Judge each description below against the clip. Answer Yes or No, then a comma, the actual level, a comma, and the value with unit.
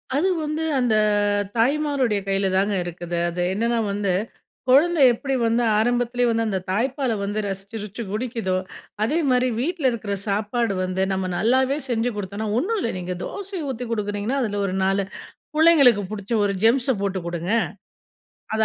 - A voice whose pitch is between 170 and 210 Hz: No, high, 225 Hz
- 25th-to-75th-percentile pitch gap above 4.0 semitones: Yes, average, 4.6 semitones